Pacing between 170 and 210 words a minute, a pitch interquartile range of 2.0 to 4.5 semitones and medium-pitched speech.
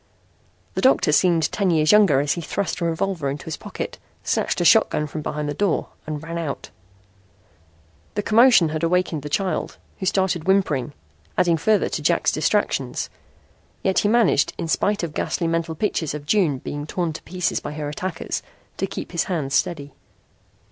Yes: average, 175 wpm; average, 4.0 semitones; medium, 165 Hz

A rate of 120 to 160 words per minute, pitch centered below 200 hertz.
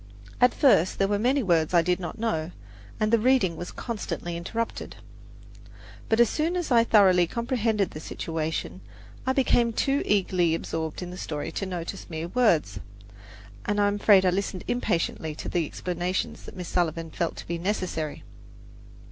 No: average, 170 wpm; medium, 185 Hz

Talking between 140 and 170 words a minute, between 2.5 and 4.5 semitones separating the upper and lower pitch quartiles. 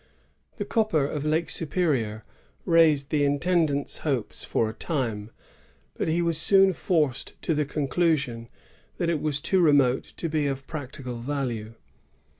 Yes: average, 150 wpm; average, 4.0 semitones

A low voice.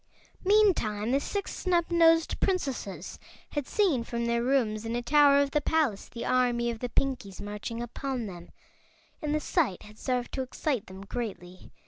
No: very high, 250 Hz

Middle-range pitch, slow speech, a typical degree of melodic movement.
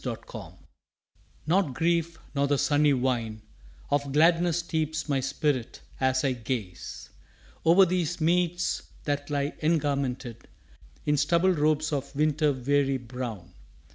Yes: medium, 145 Hz; slow, 120 wpm; average, 3.6 semitones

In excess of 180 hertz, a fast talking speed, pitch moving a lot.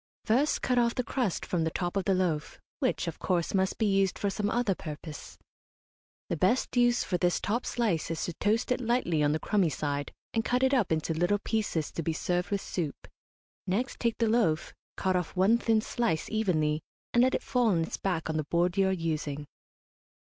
Yes: high, 190 Hz; fast, 215 wpm; wide, 5.7 semitones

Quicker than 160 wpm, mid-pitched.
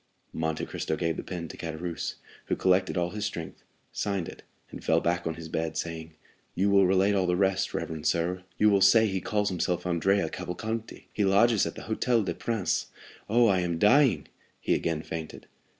No: average, 195 wpm; very low, 95 Hz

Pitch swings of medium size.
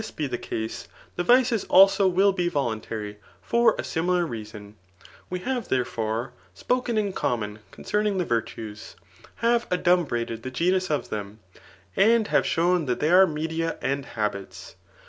No: wide, 9.0 semitones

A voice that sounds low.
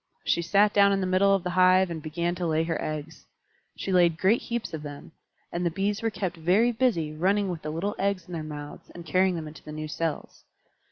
No: medium, 175 Hz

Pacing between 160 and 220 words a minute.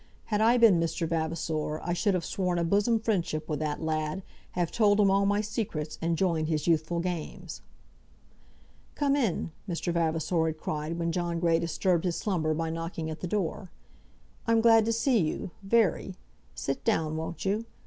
Yes: average, 180 wpm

